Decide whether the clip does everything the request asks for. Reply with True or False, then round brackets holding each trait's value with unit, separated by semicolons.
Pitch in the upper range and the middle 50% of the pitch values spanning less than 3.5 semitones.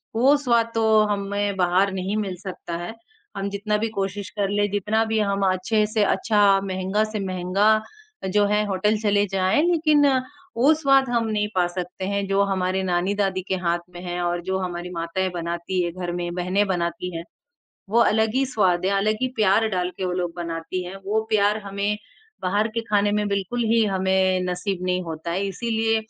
True (195 Hz; 2.7 semitones)